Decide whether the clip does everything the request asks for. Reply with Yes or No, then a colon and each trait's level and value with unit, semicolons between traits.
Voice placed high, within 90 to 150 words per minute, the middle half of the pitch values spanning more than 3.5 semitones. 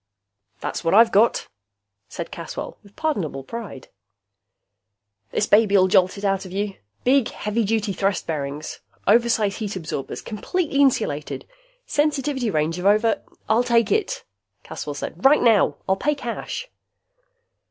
Yes: high, 210 Hz; average, 140 wpm; average, 4.1 semitones